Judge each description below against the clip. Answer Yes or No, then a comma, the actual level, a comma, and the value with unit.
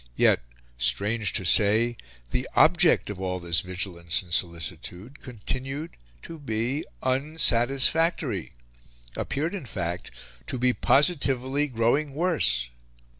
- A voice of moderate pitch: No, low, 120 Hz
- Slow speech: Yes, slow, 110 wpm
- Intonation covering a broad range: Yes, wide, 7.6 semitones